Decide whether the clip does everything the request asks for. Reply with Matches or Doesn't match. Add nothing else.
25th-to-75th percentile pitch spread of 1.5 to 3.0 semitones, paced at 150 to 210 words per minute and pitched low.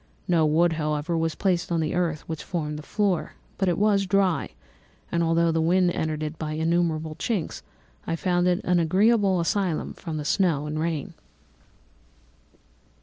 Doesn't match